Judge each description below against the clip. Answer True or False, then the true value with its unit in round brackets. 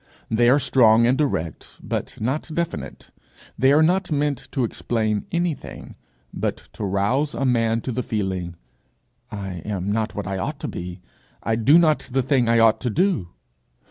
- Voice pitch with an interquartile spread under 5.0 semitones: False (5.4 semitones)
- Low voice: True (115 Hz)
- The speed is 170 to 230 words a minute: True (175 wpm)